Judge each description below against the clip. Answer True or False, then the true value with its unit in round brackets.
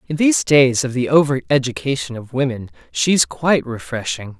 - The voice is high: False (130 Hz)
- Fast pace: False (165 wpm)